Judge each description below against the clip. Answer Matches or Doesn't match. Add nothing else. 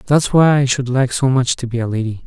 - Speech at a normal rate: Doesn't match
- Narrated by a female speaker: Doesn't match